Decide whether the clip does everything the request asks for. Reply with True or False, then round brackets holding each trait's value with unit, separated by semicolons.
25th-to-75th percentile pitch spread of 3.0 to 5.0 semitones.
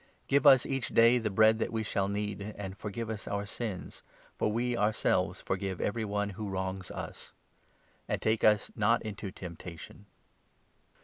False (2.4 semitones)